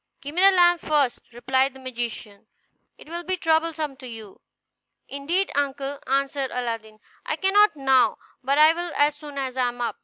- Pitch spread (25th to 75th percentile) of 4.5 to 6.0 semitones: No, average, 4.1 semitones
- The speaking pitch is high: Yes, very high, 280 Hz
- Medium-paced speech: Yes, average, 180 wpm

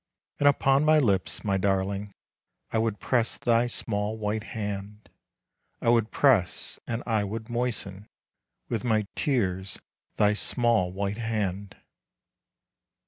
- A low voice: Yes, low, 110 Hz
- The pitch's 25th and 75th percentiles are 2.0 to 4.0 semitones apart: Yes, average, 2.9 semitones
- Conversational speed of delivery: No, slow, 125 wpm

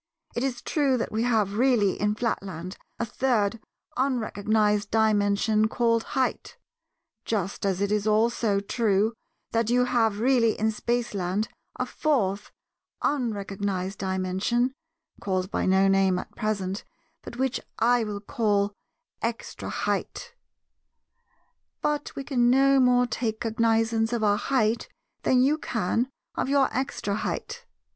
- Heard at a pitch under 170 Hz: No, high, 220 Hz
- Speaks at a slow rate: Yes, slow, 130 wpm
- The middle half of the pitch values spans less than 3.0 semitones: No, average, 3.4 semitones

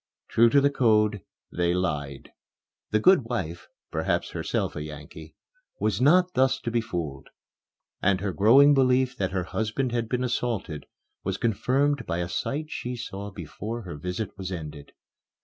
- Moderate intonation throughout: No, wide, 6.2 semitones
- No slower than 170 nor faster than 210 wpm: No, average, 160 wpm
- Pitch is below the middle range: Yes, low, 105 Hz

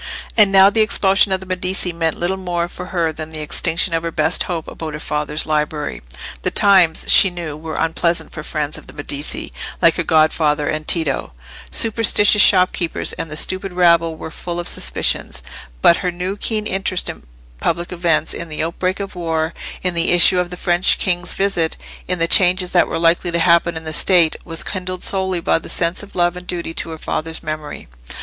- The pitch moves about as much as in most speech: No, narrow, 2.3 semitones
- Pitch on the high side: No, medium, 170 Hz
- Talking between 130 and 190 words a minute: No, average, 200 wpm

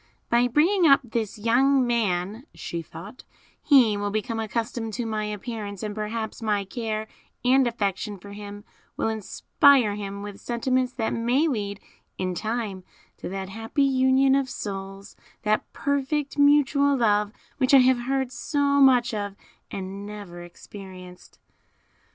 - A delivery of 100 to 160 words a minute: Yes, average, 145 wpm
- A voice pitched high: Yes, high, 225 Hz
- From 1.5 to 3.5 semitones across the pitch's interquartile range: No, average, 4.3 semitones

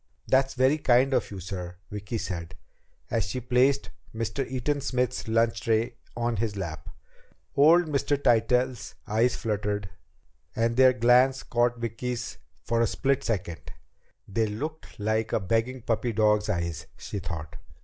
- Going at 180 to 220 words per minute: No, average, 145 wpm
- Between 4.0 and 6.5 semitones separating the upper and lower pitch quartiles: No, average, 3.5 semitones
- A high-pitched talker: No, low, 115 Hz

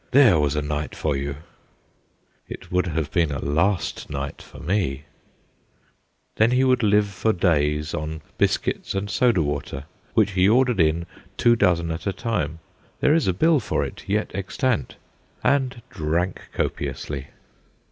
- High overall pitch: No, very low, 90 Hz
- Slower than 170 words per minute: Yes, average, 155 wpm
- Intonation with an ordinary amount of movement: No, wide, 6.4 semitones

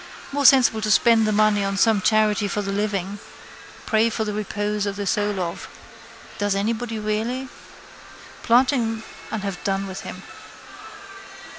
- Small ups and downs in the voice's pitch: Yes, narrow, 1.8 semitones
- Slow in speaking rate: No, average, 155 wpm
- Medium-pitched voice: No, high, 210 Hz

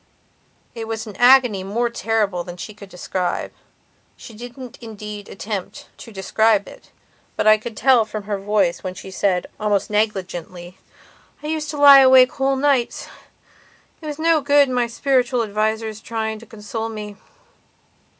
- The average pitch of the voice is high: Yes, high, 220 Hz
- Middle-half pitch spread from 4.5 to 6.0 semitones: No, average, 3.6 semitones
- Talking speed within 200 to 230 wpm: No, average, 155 wpm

